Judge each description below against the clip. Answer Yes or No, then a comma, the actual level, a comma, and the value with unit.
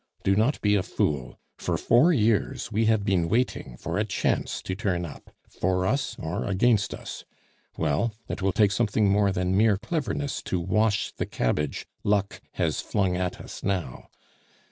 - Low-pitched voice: Yes, low, 100 Hz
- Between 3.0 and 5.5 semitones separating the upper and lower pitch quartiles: Yes, average, 3.4 semitones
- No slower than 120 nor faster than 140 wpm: No, average, 170 wpm